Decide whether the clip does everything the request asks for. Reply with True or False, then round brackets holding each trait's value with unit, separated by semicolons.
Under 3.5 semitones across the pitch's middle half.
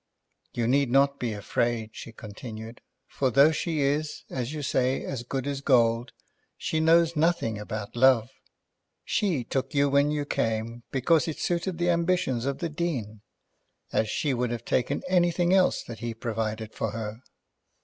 False (5.2 semitones)